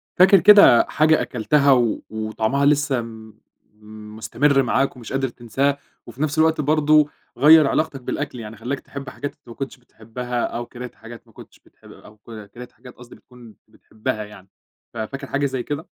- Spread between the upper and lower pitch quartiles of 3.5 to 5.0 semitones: Yes, average, 3.8 semitones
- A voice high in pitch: No, low, 125 Hz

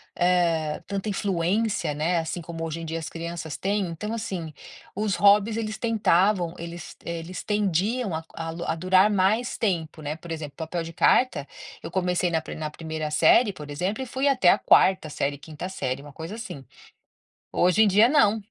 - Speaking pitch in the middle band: Yes, medium, 175 Hz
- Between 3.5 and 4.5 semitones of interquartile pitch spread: Yes, average, 4.2 semitones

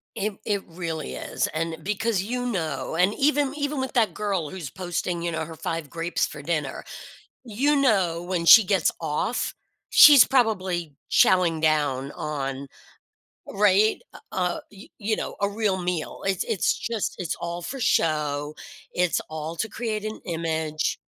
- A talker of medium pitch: Yes, medium, 180 Hz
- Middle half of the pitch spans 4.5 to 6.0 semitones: Yes, average, 5.0 semitones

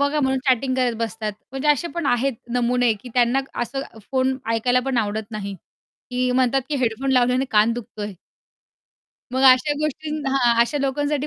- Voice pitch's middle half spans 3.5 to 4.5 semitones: No, narrow, 2.5 semitones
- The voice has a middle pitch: No, very high, 255 Hz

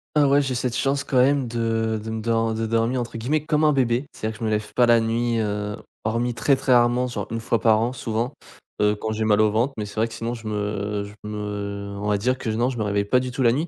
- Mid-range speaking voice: No, low, 115 Hz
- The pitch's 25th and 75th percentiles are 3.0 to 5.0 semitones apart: No, narrow, 2.5 semitones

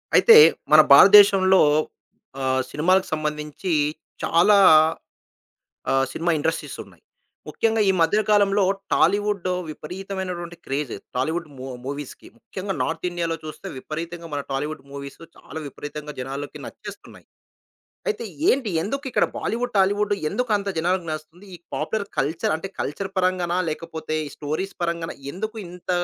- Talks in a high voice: No, medium, 175 Hz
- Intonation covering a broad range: No, average, 4.5 semitones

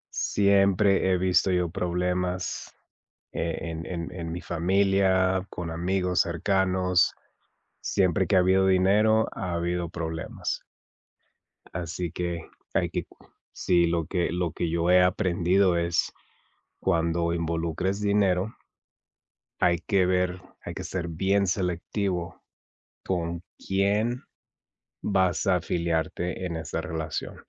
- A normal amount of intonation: No, narrow, 1.9 semitones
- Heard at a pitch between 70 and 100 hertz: Yes, very low, 90 Hz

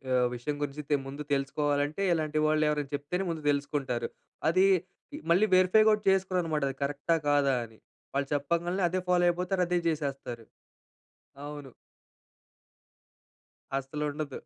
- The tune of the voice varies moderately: Yes, average, 3.8 semitones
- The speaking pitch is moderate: Yes, medium, 150 Hz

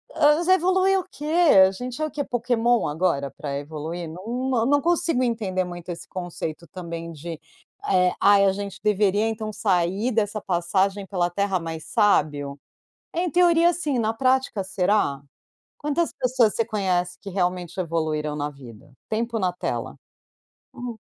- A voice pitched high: Yes, high, 200 Hz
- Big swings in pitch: Yes, wide, 6.0 semitones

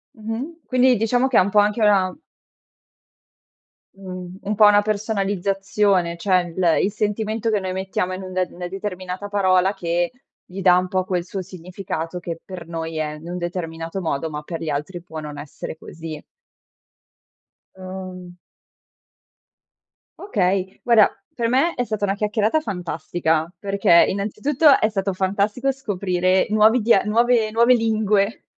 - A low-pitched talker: No, high, 190 Hz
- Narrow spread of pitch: No, average, 3.2 semitones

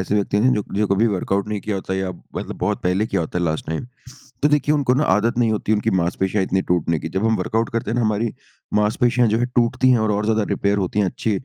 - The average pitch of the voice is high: No, low, 105 Hz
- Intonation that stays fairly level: No, average, 3.2 semitones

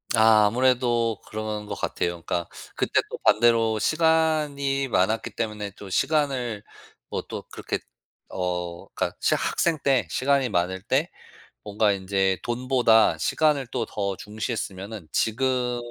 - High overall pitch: No, low, 115 Hz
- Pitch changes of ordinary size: Yes, average, 4.4 semitones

